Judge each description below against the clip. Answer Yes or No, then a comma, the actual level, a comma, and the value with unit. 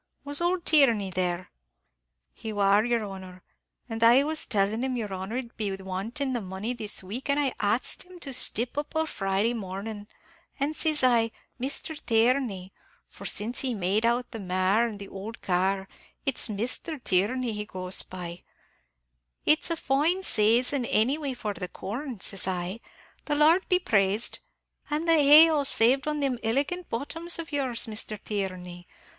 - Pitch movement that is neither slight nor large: No, wide, 6.1 semitones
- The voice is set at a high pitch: Yes, high, 230 Hz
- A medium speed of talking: Yes, average, 170 wpm